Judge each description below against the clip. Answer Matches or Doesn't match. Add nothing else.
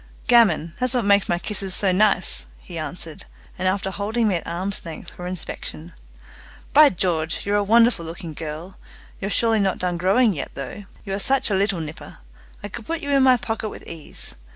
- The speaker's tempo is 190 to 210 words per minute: Matches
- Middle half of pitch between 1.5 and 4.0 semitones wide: Doesn't match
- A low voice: Doesn't match